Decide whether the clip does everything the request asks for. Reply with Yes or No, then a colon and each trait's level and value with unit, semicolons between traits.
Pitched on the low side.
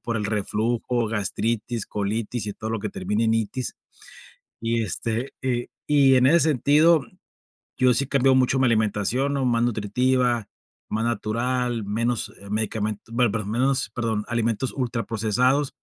Yes: low, 115 Hz